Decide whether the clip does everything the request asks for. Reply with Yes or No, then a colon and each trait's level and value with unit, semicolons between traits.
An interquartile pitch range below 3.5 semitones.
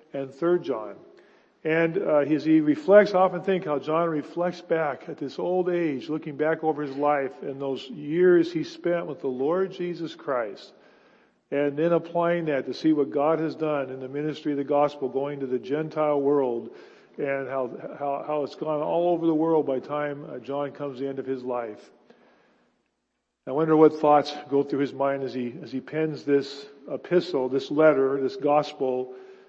Yes: narrow, 2.6 semitones